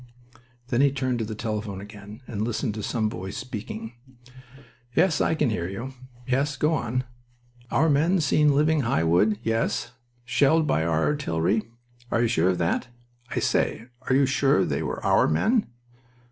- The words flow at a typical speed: Yes, average, 170 wpm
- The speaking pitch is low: Yes, low, 120 Hz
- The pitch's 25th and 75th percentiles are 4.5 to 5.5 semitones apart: Yes, average, 5.2 semitones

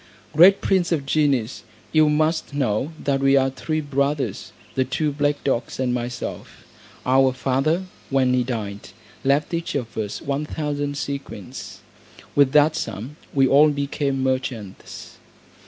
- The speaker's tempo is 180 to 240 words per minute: No, average, 140 wpm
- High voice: No, medium, 140 Hz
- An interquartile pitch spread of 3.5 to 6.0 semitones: No, narrow, 2.4 semitones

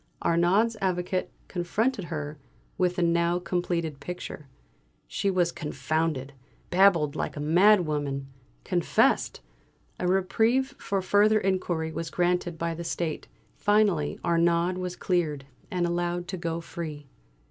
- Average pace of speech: No, slow, 125 wpm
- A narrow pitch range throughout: Yes, narrow, 2.3 semitones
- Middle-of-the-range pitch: Yes, medium, 175 Hz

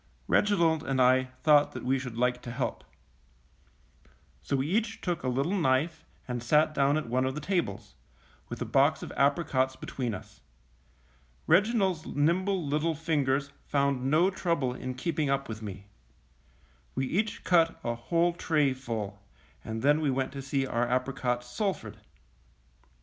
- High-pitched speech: No, medium, 140 Hz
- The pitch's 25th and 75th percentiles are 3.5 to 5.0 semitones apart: Yes, average, 4.4 semitones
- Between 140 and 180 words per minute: Yes, average, 155 wpm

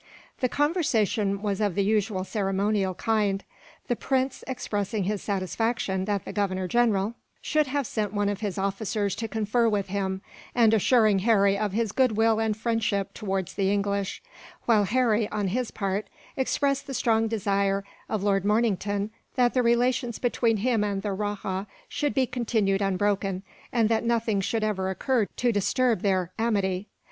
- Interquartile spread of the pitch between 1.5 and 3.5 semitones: Yes, average, 2.9 semitones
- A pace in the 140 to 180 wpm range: Yes, average, 160 wpm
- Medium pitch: No, high, 210 Hz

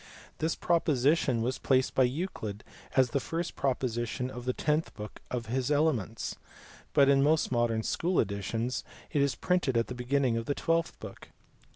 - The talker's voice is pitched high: No, low, 130 Hz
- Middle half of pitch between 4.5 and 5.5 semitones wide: No, average, 4.1 semitones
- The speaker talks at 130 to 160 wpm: No, average, 170 wpm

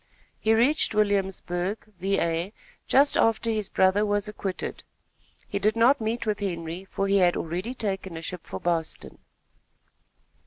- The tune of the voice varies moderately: Yes, average, 3.1 semitones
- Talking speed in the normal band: Yes, average, 145 wpm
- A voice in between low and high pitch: No, high, 200 Hz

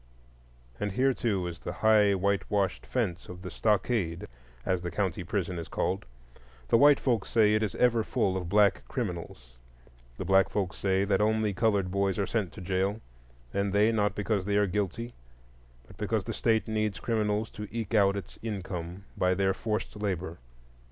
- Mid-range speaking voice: No, low, 100 Hz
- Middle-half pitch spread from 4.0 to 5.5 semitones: No, average, 2.8 semitones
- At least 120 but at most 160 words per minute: No, average, 175 wpm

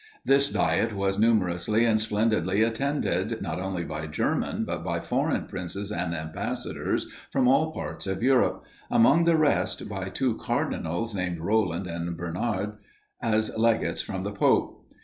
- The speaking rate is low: No, average, 150 wpm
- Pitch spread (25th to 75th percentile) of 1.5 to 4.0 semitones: No, average, 4.7 semitones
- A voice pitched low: Yes, low, 105 Hz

